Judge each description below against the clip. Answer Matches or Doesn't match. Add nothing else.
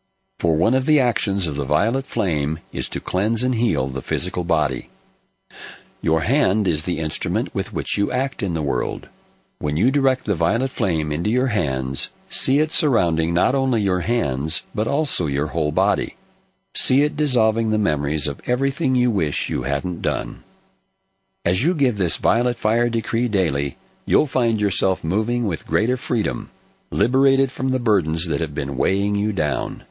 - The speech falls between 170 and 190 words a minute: Matches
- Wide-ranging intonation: Matches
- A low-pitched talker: Matches